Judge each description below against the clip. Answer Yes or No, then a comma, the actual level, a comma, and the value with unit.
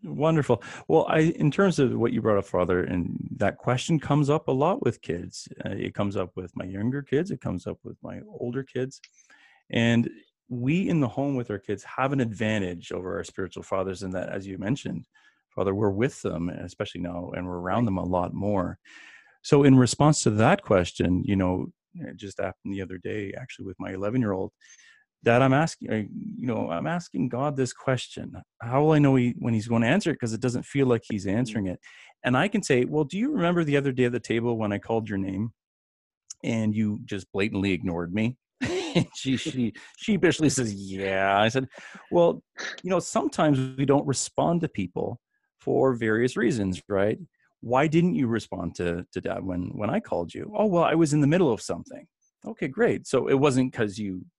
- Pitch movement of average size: No, wide, 6.1 semitones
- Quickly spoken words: Yes, fast, 210 wpm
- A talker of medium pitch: No, low, 115 Hz